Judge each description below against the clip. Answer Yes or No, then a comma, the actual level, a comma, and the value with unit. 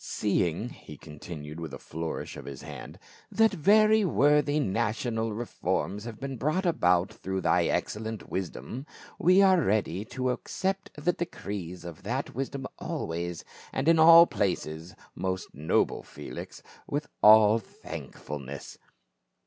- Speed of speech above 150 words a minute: No, slow, 135 wpm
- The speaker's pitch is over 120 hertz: No, low, 110 Hz